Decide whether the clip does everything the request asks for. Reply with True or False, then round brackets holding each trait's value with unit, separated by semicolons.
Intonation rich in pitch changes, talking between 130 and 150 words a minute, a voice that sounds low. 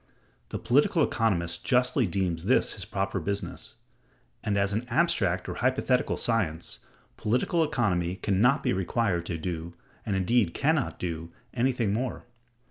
True (5.7 semitones; 145 wpm; 100 Hz)